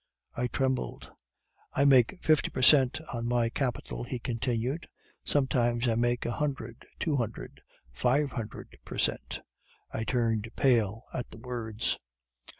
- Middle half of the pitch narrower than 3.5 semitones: Yes, narrow, 2.4 semitones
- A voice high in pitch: No, low, 120 Hz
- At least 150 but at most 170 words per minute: No, average, 140 wpm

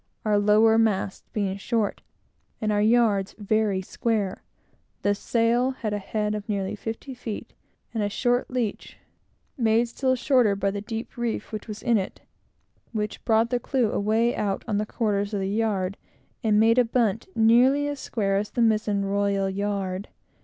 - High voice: Yes, high, 215 Hz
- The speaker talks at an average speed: Yes, average, 170 wpm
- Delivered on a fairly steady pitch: Yes, narrow, 2.3 semitones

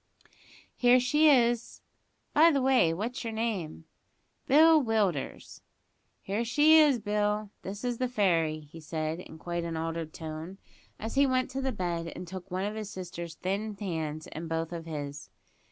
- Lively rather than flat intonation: Yes, wide, 6.8 semitones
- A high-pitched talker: Yes, high, 195 Hz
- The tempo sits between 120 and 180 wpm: Yes, average, 170 wpm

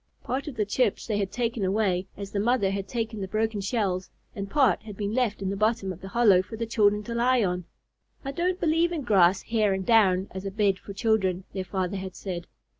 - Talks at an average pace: No, fast, 235 wpm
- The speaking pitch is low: No, high, 205 Hz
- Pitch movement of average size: Yes, average, 3.3 semitones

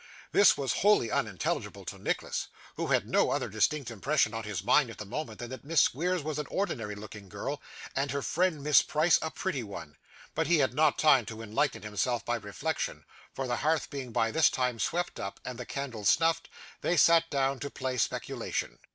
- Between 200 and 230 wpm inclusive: Yes, fast, 205 wpm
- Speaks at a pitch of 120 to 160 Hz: Yes, low, 135 Hz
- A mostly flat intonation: No, wide, 5.5 semitones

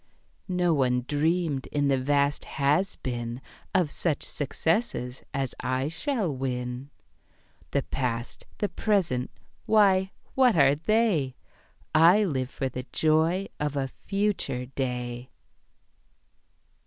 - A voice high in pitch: No, medium, 145 Hz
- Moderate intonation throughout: No, wide, 5.7 semitones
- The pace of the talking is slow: Yes, slow, 115 wpm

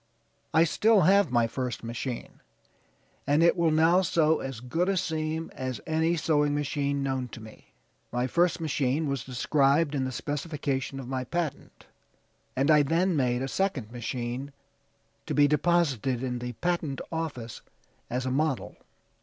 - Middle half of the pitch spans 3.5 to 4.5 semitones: Yes, average, 4.1 semitones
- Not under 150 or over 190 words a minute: Yes, average, 155 wpm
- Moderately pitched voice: Yes, medium, 145 Hz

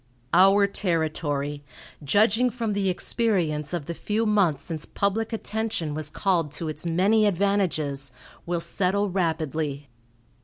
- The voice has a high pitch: No, medium, 180 Hz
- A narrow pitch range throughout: No, average, 4.8 semitones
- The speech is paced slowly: Yes, slow, 125 wpm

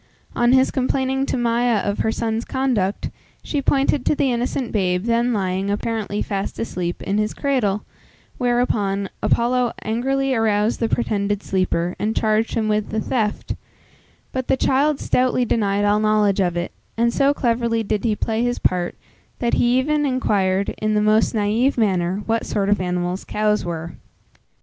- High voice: Yes, high, 220 Hz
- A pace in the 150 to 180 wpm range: Yes, average, 165 wpm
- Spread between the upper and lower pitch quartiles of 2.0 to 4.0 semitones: Yes, average, 3.5 semitones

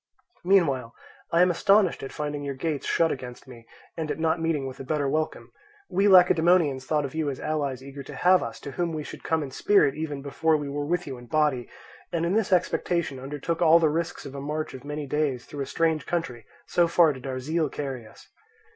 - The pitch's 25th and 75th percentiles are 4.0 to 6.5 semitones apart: No, average, 3.5 semitones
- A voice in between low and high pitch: Yes, medium, 150 Hz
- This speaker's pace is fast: Yes, fast, 225 wpm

